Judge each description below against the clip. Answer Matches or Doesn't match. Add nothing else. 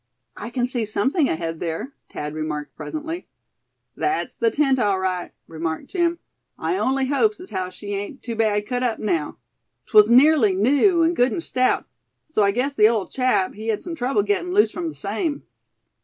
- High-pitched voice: Matches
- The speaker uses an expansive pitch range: Matches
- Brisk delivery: Doesn't match